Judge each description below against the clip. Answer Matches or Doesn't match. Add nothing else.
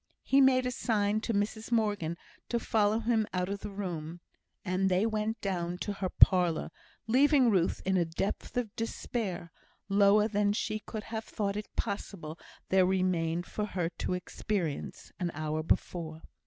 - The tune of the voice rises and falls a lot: Doesn't match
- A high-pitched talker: Matches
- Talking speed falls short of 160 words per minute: Doesn't match